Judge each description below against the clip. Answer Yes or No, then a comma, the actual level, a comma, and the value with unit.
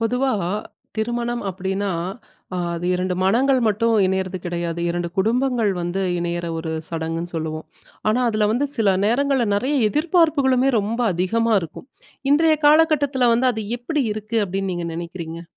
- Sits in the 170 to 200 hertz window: No, high, 215 Hz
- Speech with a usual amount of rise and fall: No, wide, 6.4 semitones